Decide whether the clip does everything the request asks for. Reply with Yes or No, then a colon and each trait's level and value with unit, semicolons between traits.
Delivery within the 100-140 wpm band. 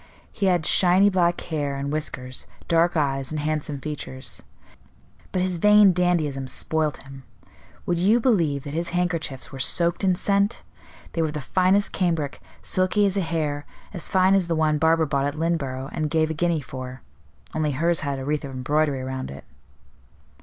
No: average, 180 wpm